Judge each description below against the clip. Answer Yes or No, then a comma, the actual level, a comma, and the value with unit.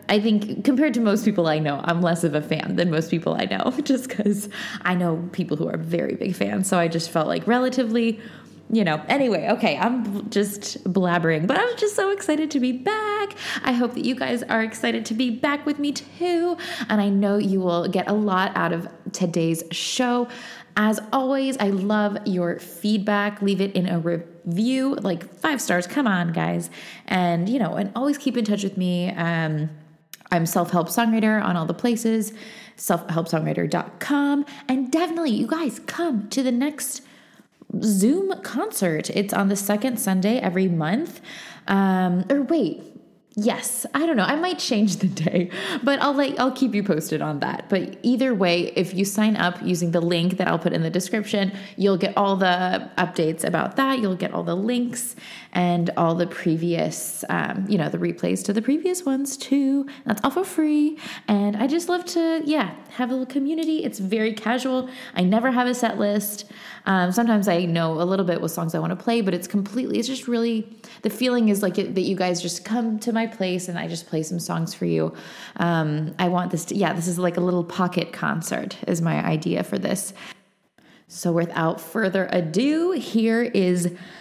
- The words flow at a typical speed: Yes, average, 195 wpm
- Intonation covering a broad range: Yes, wide, 6.0 semitones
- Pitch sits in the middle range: No, high, 205 Hz